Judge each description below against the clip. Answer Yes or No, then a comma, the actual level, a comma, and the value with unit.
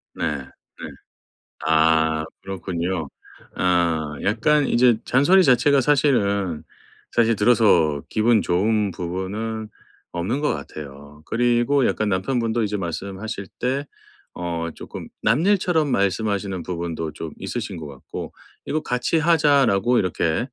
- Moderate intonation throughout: No, wide, 6.3 semitones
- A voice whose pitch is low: Yes, low, 100 Hz